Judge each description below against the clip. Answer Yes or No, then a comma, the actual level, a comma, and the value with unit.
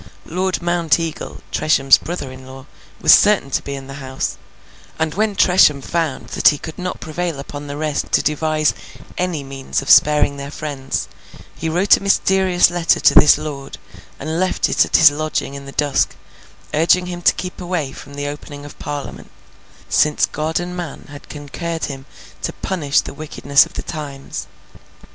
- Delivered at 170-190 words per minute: Yes, average, 175 wpm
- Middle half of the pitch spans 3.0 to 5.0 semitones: Yes, average, 3.6 semitones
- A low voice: No, medium, 155 Hz